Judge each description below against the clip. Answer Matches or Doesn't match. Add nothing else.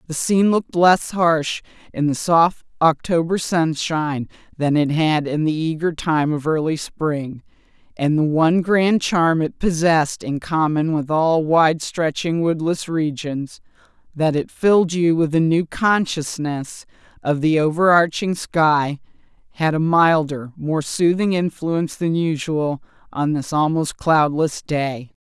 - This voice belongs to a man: Doesn't match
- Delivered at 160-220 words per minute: Doesn't match